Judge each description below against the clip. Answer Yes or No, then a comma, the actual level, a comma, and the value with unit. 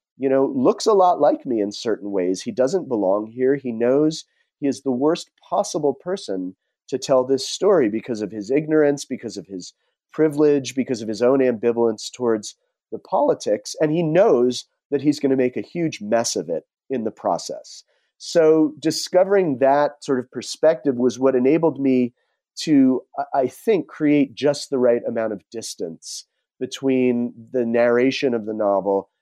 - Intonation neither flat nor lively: Yes, average, 4.0 semitones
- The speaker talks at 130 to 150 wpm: No, average, 175 wpm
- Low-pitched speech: Yes, low, 130 Hz